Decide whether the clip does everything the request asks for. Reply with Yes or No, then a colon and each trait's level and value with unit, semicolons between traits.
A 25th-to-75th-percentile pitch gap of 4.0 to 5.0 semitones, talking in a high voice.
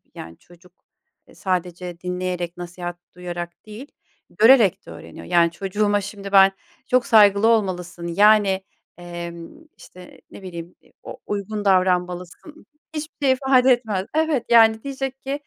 Yes: average, 4.3 semitones; high, 195 Hz